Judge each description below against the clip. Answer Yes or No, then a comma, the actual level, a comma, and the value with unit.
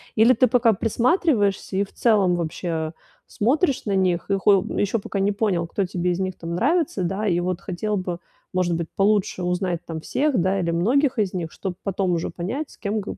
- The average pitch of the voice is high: Yes, high, 195 Hz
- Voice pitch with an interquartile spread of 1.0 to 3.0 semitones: No, average, 3.7 semitones